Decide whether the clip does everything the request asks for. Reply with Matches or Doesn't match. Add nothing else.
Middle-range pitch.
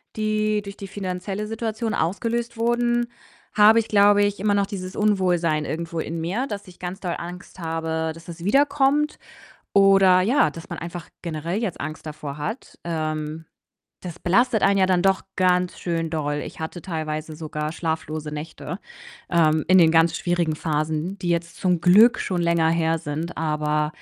Matches